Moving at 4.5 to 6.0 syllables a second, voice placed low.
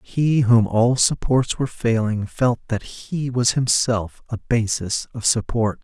No: 3.8 syllables/s; low, 120 Hz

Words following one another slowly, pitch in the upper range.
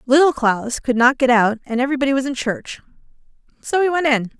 No: fast, 205 wpm; very high, 260 Hz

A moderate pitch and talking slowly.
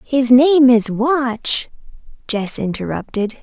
No: high, 245 Hz; slow, 105 wpm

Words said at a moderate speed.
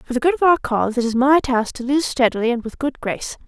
No: fast, 295 wpm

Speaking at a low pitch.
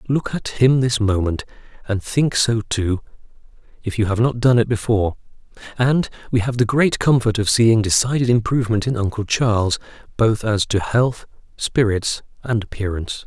Yes: low, 115 Hz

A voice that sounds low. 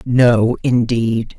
Yes: low, 120 Hz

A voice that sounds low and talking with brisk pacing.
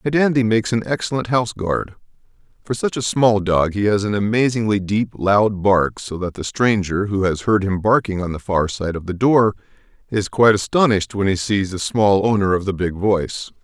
Yes: low, 105 Hz; fast, 210 wpm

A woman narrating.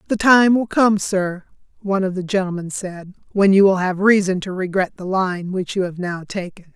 Yes: female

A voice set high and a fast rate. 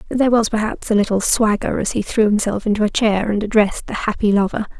Yes: high, 215 Hz; fast, 225 wpm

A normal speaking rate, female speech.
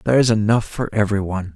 No: average, 155 wpm; male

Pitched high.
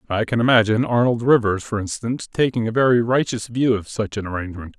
No: low, 115 Hz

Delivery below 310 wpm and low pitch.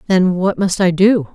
No: fast, 220 wpm; medium, 185 Hz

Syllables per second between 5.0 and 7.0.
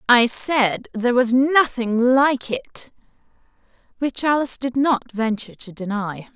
No: 4.3 syllables/s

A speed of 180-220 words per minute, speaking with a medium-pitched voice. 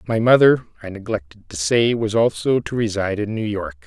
No: average, 200 wpm; low, 115 Hz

